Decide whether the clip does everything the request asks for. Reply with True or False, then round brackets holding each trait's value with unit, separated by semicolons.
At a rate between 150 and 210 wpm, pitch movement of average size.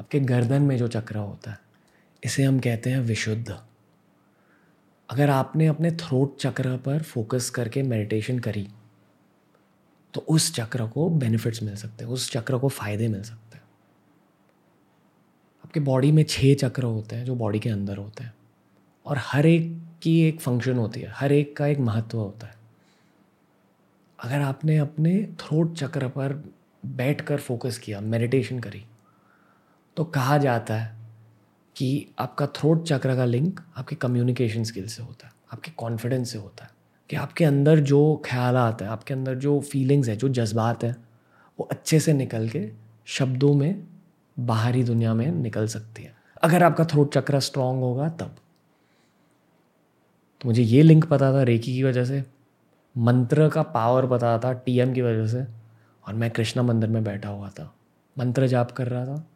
True (165 wpm; 3.8 semitones)